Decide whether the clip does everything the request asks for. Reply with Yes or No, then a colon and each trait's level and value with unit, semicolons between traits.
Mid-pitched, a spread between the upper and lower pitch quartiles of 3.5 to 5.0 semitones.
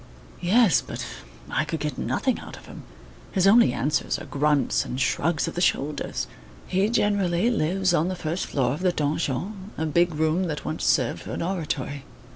Yes: medium, 165 Hz; average, 4.0 semitones